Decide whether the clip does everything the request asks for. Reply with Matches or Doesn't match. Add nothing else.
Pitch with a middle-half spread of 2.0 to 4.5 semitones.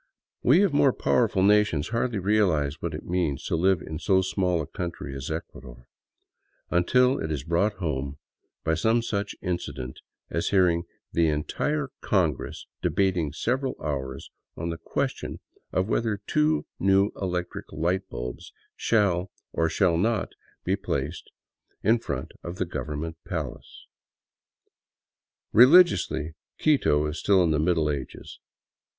Doesn't match